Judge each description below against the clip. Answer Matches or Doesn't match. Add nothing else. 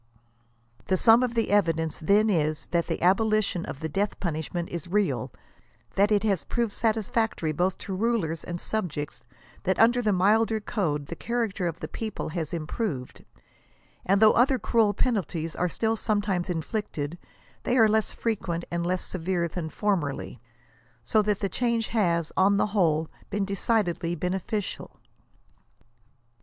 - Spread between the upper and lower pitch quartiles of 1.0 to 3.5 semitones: Doesn't match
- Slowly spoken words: Doesn't match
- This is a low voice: Doesn't match